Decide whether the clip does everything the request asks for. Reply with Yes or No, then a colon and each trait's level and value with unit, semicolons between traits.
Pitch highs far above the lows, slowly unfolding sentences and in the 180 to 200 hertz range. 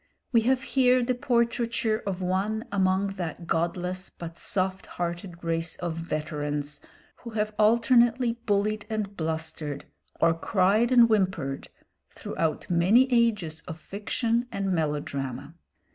Yes: wide, 5.7 semitones; slow, 125 wpm; high, 190 Hz